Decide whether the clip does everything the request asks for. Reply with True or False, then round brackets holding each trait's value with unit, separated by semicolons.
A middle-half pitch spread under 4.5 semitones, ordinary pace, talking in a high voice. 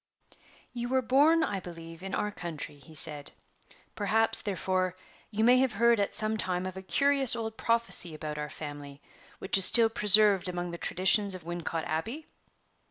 False (4.9 semitones; 170 wpm; 195 Hz)